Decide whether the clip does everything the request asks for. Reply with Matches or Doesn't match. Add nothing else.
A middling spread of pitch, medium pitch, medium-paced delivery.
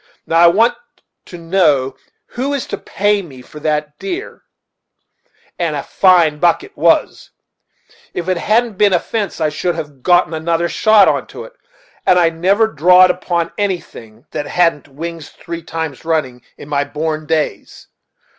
Matches